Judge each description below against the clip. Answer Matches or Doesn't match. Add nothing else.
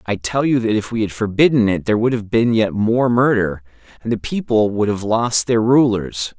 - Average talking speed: Doesn't match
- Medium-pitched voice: Doesn't match